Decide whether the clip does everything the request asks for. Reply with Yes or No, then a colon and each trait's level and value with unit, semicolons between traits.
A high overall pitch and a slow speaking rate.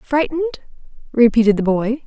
Yes: very high, 255 Hz; slow, 115 wpm